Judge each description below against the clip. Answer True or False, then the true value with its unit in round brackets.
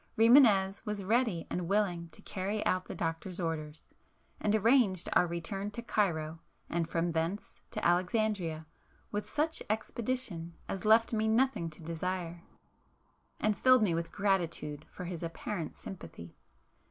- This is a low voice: False (185 Hz)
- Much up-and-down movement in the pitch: False (4.4 semitones)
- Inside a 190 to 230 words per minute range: False (140 wpm)